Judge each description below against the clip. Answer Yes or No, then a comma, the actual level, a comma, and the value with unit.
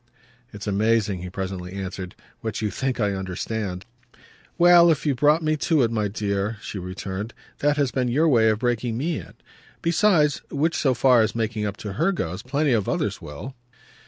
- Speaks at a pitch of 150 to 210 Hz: No, low, 115 Hz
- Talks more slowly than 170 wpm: No, average, 190 wpm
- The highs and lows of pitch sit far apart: Yes, wide, 6.4 semitones